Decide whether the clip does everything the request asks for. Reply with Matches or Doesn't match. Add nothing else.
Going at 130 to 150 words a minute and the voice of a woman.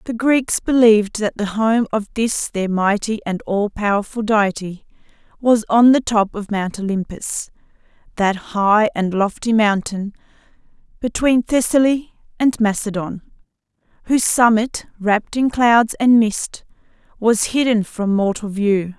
Matches